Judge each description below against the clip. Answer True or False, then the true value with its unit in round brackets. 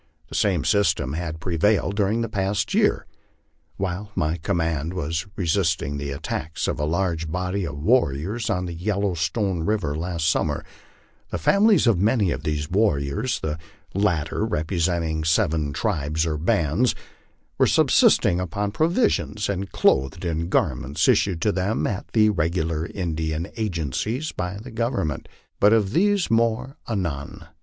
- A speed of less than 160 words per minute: True (150 wpm)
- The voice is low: True (90 Hz)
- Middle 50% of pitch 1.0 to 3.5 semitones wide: False (4.7 semitones)